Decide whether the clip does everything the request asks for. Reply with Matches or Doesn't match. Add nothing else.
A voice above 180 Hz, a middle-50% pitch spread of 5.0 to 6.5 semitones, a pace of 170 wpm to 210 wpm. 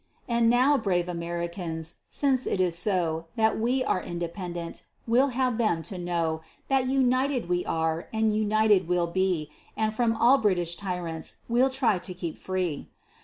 Doesn't match